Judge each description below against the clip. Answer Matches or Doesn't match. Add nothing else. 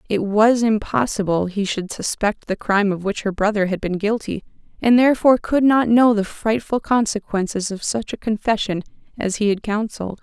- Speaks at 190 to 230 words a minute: Doesn't match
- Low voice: Doesn't match